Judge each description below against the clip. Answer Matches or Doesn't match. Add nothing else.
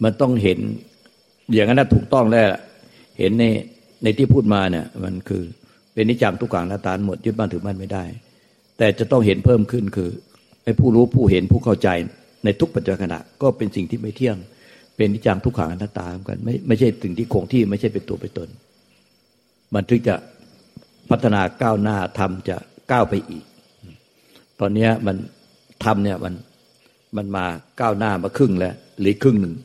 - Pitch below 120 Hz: Matches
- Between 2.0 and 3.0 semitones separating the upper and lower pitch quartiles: Doesn't match